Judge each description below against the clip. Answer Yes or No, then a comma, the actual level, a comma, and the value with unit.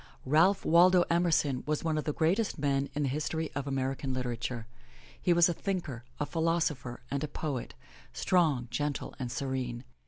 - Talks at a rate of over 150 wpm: Yes, average, 165 wpm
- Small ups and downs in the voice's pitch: No, average, 4.1 semitones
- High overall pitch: No, medium, 145 Hz